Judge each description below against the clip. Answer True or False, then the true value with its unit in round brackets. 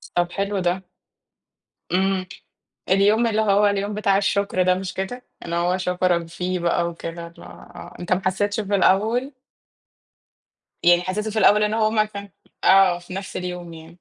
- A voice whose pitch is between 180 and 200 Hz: True (190 Hz)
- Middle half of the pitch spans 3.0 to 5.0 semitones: False (2.6 semitones)